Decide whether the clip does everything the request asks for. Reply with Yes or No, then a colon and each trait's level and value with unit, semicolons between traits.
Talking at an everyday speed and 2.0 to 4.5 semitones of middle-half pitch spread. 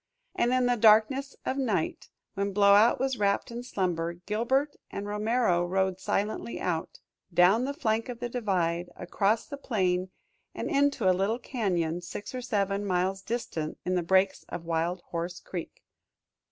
No: average, 160 wpm; average, 4.9 semitones